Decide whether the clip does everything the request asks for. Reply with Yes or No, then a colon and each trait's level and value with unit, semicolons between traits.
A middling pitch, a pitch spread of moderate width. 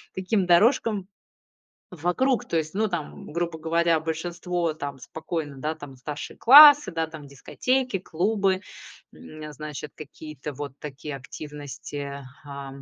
Yes: medium, 160 Hz; average, 4.0 semitones